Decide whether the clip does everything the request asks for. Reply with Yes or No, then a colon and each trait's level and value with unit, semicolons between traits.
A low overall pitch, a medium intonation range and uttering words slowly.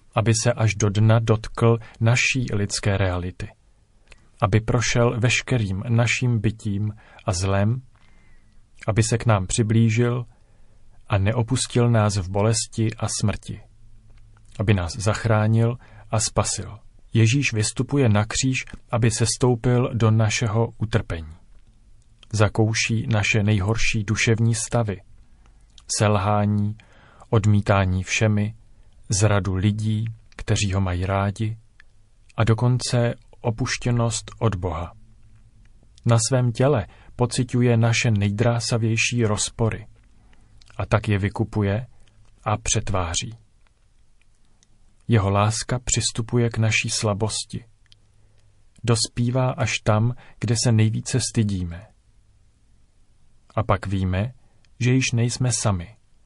No: low, 110 Hz; narrow, 1.9 semitones; slow, 100 wpm